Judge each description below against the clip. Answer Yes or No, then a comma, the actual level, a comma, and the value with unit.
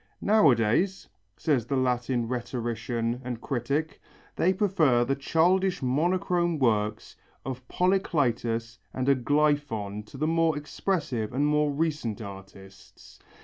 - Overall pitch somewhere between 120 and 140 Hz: Yes, low, 135 Hz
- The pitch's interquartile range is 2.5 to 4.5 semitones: No, average, 5.3 semitones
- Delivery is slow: Yes, slow, 110 wpm